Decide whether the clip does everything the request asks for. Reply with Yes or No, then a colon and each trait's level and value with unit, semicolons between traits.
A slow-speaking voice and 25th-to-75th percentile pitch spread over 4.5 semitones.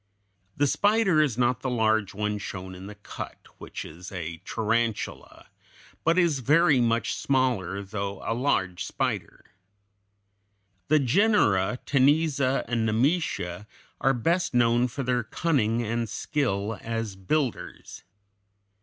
Yes: slow, 125 wpm; wide, 5.4 semitones